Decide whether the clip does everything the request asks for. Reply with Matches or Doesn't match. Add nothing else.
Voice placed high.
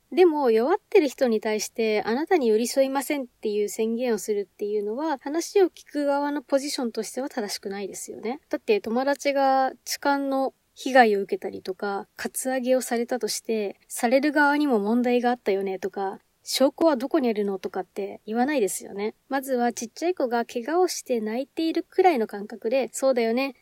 Matches